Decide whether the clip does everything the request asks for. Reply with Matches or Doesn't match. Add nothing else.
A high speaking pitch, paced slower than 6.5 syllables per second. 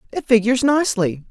Doesn't match